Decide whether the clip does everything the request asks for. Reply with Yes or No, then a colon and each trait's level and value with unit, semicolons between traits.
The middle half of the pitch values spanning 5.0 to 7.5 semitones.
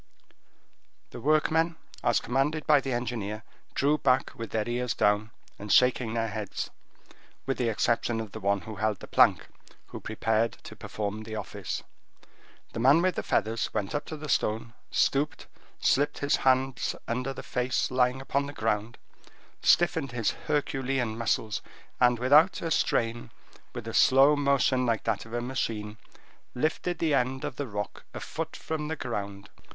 No: average, 3.9 semitones